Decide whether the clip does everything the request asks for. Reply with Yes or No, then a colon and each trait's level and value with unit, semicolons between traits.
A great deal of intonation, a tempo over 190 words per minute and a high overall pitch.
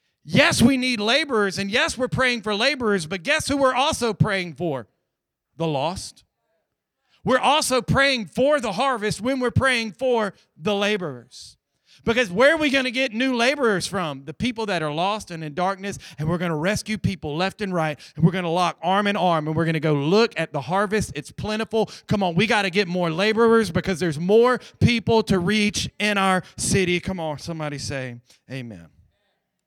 Yes: wide, 5.9 semitones; average, 200 wpm; high, 200 Hz